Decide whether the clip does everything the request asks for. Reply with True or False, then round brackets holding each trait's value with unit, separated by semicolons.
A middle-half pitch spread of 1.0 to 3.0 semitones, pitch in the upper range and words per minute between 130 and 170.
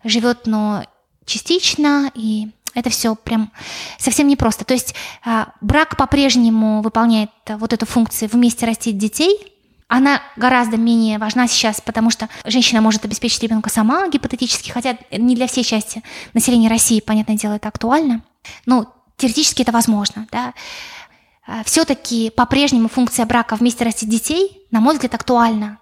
True (2.5 semitones; 235 Hz; 140 wpm)